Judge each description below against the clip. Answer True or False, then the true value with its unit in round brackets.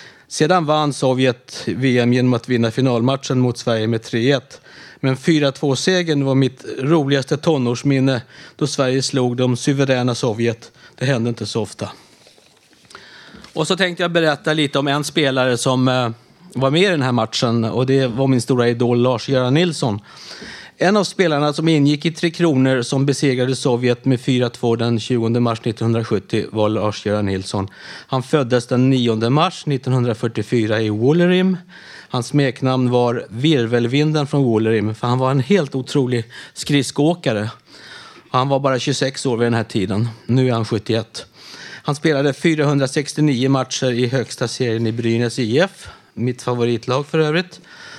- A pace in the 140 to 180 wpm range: True (150 wpm)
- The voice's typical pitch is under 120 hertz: False (130 Hz)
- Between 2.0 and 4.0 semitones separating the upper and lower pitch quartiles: True (3.3 semitones)